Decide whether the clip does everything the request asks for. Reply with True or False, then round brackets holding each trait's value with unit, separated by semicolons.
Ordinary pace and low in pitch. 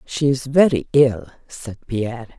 True (150 wpm; 125 Hz)